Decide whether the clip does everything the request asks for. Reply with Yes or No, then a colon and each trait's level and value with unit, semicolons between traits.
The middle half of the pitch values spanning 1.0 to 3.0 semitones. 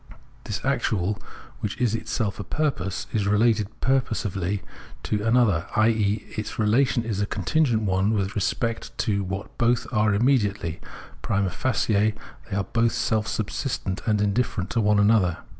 Yes: narrow, 2.5 semitones